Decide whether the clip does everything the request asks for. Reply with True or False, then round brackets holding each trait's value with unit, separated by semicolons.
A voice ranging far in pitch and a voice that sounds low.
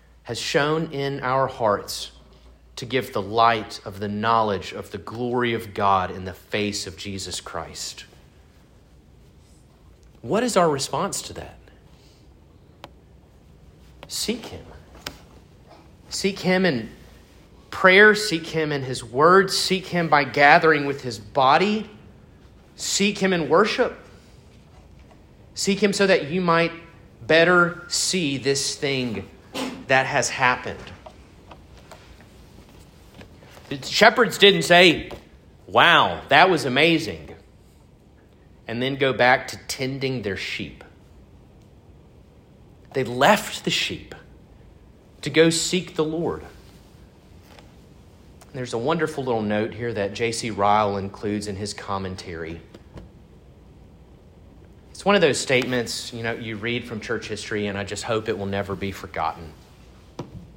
True (7.6 semitones; 115 Hz)